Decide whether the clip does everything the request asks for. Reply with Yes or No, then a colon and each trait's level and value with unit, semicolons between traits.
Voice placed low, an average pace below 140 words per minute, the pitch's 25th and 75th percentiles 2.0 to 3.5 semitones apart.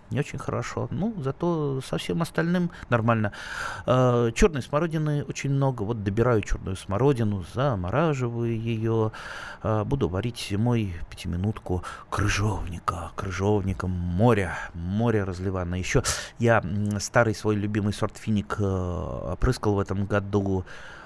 No: low, 110 Hz; average, 120 wpm; average, 3.9 semitones